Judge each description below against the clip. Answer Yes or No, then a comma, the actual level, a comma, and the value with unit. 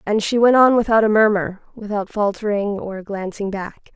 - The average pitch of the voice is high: Yes, high, 210 Hz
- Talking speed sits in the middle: Yes, average, 180 wpm